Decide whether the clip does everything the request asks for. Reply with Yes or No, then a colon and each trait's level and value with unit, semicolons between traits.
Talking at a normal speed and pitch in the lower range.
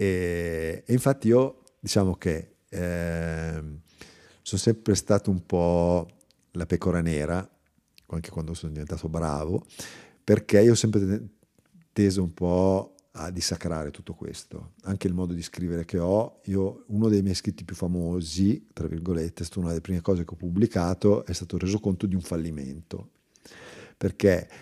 Yes: average, 155 wpm; very low, 90 Hz